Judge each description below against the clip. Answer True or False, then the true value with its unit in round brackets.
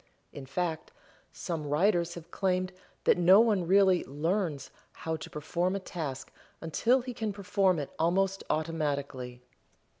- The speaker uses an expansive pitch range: False (4.2 semitones)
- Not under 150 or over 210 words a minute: False (140 wpm)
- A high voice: False (175 Hz)